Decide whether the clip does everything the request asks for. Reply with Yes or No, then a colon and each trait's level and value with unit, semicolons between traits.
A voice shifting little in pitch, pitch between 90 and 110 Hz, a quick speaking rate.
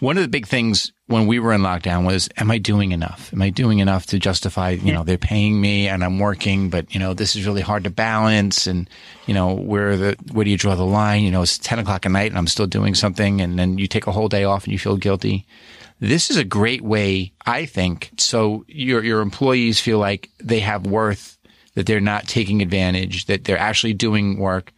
Yes: narrow, 2.2 semitones; low, 100 Hz; fast, 240 wpm